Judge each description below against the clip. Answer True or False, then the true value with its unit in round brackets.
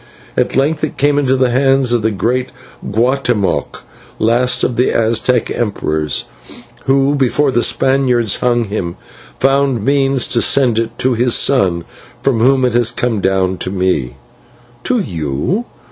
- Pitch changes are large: False (3.8 semitones)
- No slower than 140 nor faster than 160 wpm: True (150 wpm)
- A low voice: True (120 Hz)